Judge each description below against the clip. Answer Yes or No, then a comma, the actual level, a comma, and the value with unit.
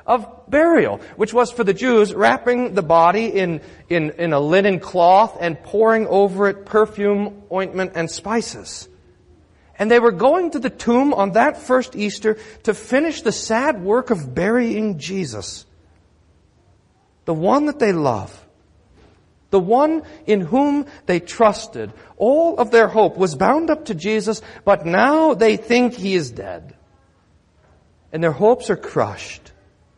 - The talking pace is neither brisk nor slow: Yes, average, 150 wpm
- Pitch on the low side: No, high, 200 Hz